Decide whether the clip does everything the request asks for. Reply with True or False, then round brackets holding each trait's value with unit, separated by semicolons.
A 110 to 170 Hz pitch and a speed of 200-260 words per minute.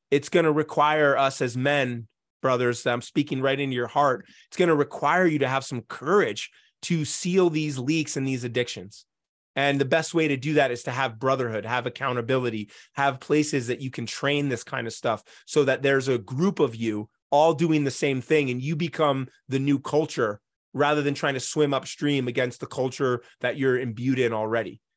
True (135 Hz; 205 wpm)